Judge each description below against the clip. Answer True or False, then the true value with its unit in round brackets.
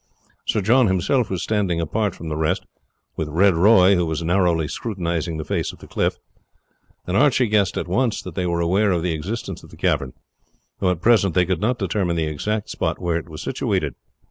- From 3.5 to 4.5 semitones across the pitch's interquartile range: True (4.0 semitones)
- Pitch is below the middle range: True (90 Hz)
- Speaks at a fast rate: True (210 wpm)